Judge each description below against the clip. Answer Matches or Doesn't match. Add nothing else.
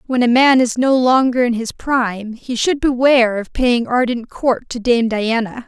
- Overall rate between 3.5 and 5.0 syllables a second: Matches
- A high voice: Matches